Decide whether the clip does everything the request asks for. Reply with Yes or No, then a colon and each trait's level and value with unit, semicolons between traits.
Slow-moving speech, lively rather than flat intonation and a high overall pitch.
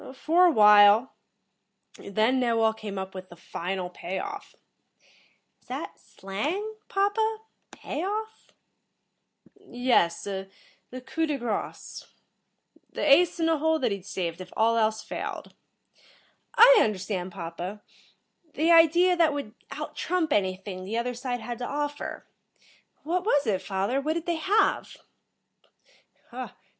Yes: slow, 130 wpm; wide, 8.7 semitones; high, 245 Hz